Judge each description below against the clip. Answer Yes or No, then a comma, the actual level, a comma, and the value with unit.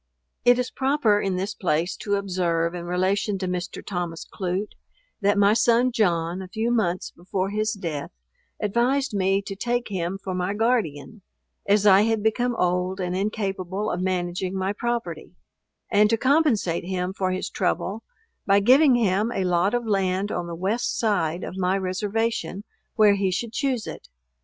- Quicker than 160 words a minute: Yes, average, 170 wpm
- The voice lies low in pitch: No, high, 195 Hz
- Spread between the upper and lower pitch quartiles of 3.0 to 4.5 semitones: Yes, average, 3.4 semitones